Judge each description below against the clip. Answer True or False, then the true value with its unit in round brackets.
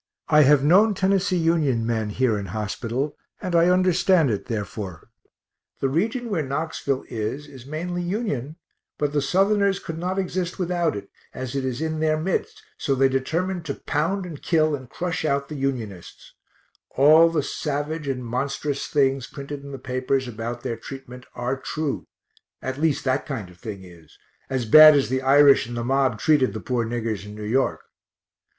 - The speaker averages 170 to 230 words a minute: True (180 wpm)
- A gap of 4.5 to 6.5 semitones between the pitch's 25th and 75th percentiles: True (4.8 semitones)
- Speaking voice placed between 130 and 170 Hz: True (140 Hz)